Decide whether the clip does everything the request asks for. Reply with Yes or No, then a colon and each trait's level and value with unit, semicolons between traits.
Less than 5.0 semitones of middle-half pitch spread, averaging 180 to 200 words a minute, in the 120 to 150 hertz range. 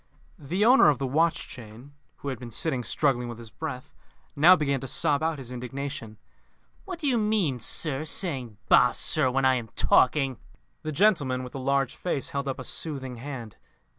Yes: average, 3.6 semitones; average, 195 wpm; low, 135 Hz